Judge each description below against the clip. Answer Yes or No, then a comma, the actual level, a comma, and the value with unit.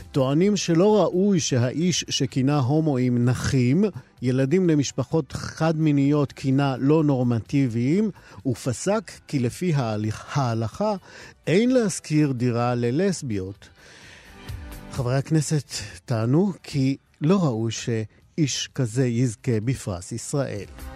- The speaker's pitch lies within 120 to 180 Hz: Yes, low, 135 Hz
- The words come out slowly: Yes, slow, 95 wpm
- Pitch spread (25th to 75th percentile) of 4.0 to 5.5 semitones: Yes, average, 5.1 semitones